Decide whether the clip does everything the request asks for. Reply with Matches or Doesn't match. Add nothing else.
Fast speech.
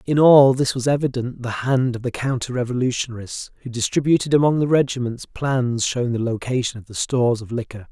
Doesn't match